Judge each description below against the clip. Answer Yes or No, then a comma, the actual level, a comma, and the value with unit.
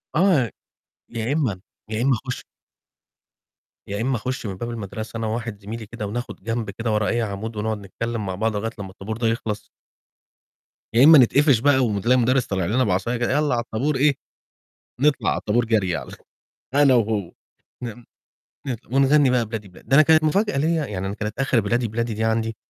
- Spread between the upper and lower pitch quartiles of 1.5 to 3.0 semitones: No, average, 3.5 semitones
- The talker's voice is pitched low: Yes, low, 115 Hz